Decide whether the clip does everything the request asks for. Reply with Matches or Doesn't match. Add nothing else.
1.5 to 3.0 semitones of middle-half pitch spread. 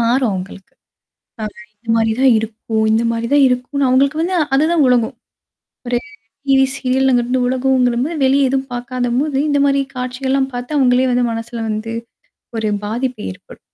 Matches